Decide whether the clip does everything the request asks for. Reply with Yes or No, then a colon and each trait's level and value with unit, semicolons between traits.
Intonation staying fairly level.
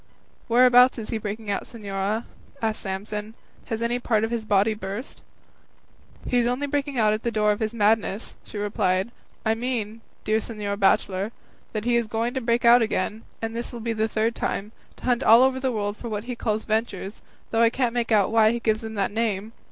Yes: narrow, 2.0 semitones